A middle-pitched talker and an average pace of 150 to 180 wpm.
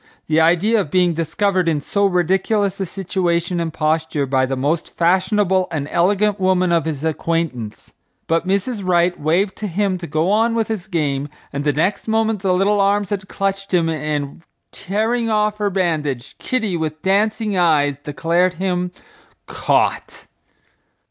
Yes: medium, 180 Hz; average, 160 wpm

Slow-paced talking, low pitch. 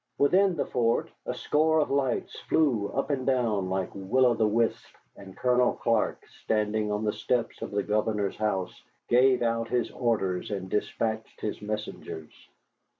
No: average, 160 wpm; low, 115 Hz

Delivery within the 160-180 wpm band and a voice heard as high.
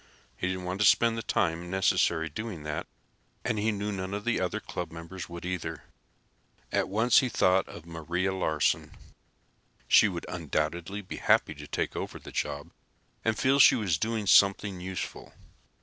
No: average, 170 wpm; very low, 95 Hz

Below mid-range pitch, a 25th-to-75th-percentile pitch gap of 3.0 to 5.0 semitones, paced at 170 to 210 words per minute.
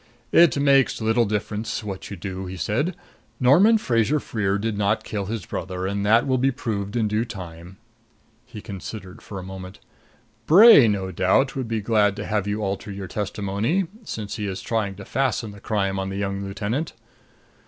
Yes: low, 105 Hz; average, 3.4 semitones; average, 185 wpm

